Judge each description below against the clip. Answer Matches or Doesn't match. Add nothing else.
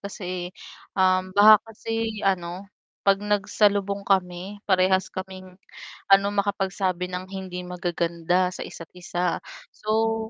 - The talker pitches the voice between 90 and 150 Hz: Doesn't match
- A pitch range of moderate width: Doesn't match